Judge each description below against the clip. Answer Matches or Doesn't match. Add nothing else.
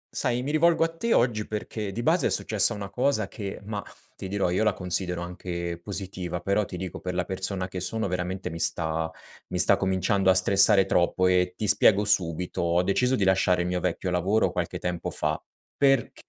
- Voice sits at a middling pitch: Doesn't match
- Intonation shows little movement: Doesn't match